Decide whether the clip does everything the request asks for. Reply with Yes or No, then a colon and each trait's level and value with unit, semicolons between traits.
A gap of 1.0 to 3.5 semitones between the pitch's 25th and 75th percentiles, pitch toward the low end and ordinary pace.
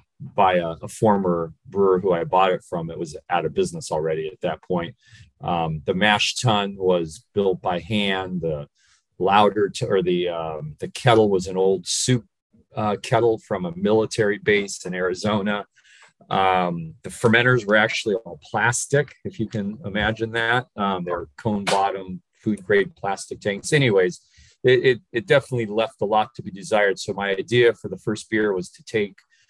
No: average, 3.9 semitones; low, 105 Hz; average, 180 wpm